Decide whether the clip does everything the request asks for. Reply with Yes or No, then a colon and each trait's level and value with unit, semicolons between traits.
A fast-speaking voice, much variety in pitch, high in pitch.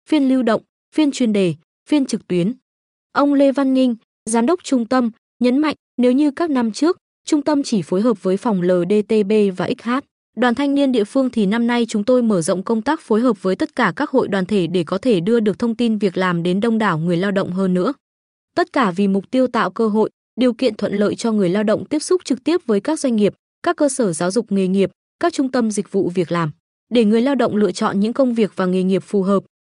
No: fast, 255 wpm; average, 5.0 semitones; high, 230 Hz